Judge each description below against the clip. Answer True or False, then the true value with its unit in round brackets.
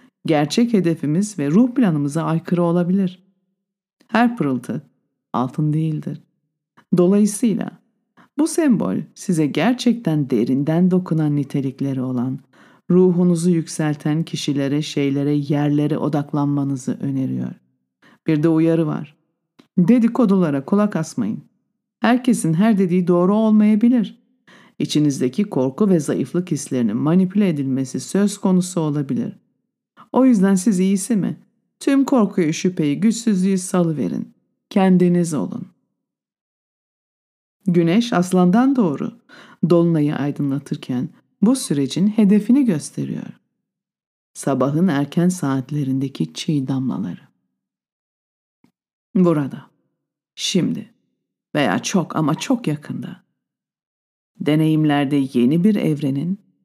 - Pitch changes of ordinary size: False (6.2 semitones)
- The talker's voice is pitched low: False (175 Hz)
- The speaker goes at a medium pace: False (90 wpm)